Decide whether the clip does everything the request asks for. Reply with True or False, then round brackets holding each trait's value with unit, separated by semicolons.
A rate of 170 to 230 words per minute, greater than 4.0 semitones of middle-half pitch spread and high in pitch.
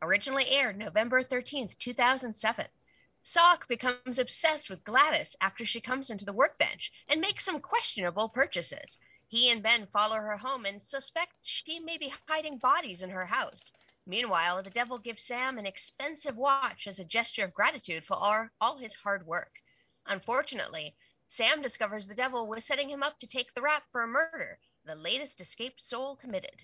True (175 wpm; 4.8 semitones; 250 Hz)